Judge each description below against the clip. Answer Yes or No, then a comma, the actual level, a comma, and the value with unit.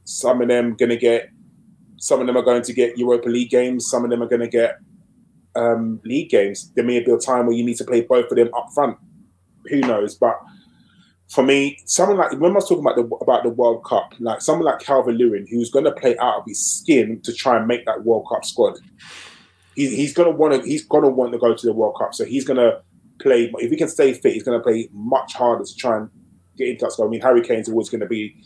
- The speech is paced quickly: Yes, fast, 255 wpm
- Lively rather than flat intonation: Yes, wide, 7.2 semitones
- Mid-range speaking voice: No, low, 125 Hz